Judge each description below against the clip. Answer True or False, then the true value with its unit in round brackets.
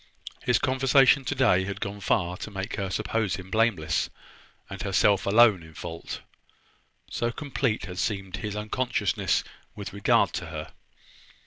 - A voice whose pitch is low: True (100 Hz)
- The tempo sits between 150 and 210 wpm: False (140 wpm)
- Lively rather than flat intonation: False (3.9 semitones)